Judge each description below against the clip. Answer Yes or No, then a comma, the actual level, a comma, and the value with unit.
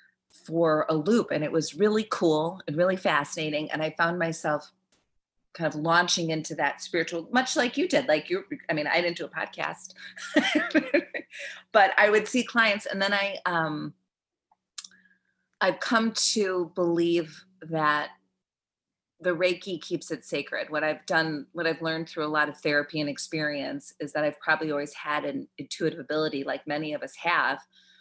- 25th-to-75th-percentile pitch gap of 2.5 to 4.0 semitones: No, average, 4.4 semitones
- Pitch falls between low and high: Yes, medium, 165 Hz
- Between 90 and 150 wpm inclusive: No, average, 170 wpm